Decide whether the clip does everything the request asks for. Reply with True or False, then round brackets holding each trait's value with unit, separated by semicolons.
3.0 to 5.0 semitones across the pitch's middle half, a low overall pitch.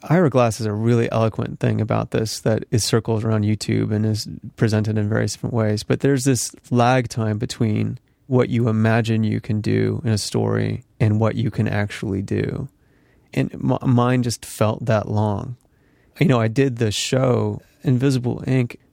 False (2.6 semitones; 115 Hz)